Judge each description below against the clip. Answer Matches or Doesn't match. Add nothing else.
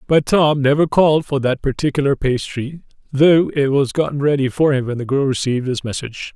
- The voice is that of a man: Matches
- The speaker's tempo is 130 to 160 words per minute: Doesn't match